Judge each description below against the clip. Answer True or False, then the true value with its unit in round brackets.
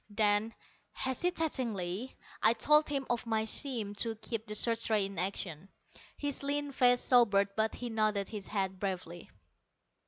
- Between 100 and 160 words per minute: True (150 wpm)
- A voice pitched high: True (220 Hz)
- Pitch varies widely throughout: False (3.8 semitones)